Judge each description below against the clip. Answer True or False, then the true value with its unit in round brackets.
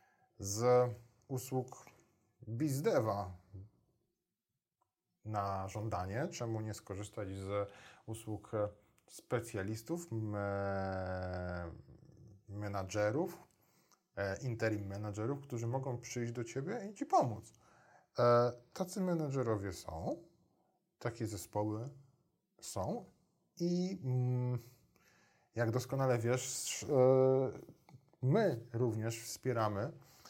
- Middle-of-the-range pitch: False (120 Hz)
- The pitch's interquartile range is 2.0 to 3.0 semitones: False (4.1 semitones)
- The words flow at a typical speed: False (70 wpm)